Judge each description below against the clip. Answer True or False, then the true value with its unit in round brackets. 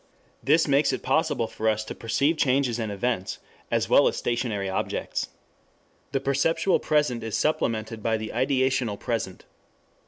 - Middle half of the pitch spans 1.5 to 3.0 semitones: False (4.0 semitones)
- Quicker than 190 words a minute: False (150 wpm)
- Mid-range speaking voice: False (120 Hz)